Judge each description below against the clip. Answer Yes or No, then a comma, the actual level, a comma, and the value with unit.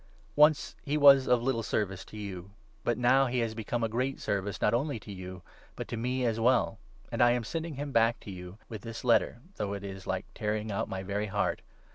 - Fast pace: Yes, fast, 240 wpm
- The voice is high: No, low, 115 Hz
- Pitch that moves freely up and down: No, average, 3.7 semitones